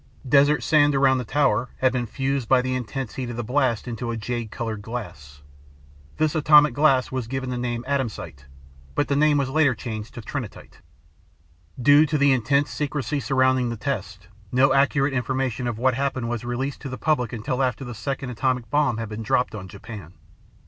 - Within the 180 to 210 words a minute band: Yes, average, 190 wpm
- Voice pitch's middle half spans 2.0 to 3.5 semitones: Yes, average, 3.0 semitones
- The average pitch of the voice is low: Yes, low, 130 Hz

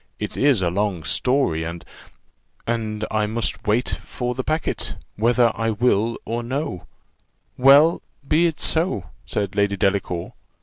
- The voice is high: No, low, 115 Hz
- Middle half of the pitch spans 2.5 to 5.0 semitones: Yes, average, 4.4 semitones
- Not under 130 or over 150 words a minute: Yes, average, 145 wpm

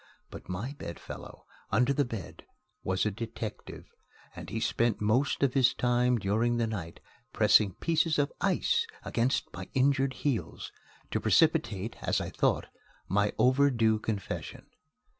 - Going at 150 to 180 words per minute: No, average, 140 wpm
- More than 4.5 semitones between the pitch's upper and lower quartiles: No, average, 4.0 semitones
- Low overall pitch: Yes, low, 120 Hz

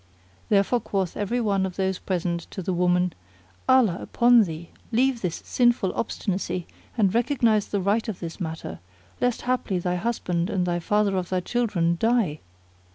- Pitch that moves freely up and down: No, average, 4.5 semitones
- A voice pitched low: No, high, 195 Hz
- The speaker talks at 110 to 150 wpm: No, average, 160 wpm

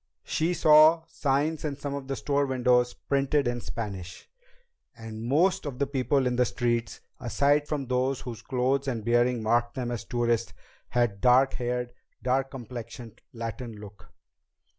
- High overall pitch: No, low, 125 Hz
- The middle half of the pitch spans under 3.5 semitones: Yes, average, 2.8 semitones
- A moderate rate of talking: Yes, average, 160 wpm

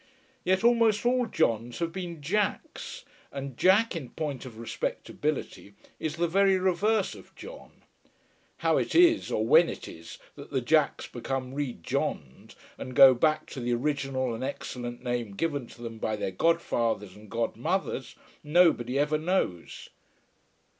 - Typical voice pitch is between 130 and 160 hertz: Yes, medium, 140 Hz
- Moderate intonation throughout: No, wide, 6.9 semitones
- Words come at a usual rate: Yes, average, 150 wpm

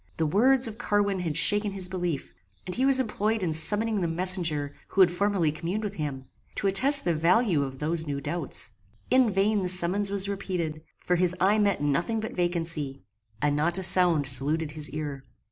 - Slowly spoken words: No, average, 195 wpm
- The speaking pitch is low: No, medium, 180 Hz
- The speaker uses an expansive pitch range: No, average, 4.6 semitones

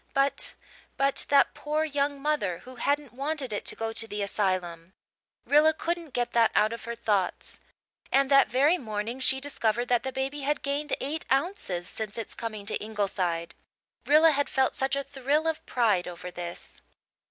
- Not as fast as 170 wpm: No, average, 175 wpm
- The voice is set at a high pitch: Yes, very high, 255 Hz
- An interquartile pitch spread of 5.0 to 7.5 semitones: Yes, average, 5.3 semitones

